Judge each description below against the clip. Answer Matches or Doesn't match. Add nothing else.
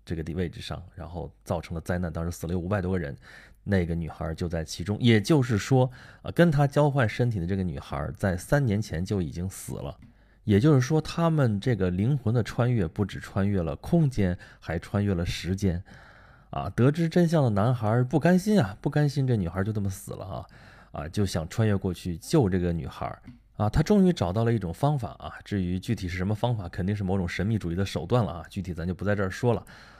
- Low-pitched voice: Matches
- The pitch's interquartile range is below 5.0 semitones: Doesn't match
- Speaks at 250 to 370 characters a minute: Matches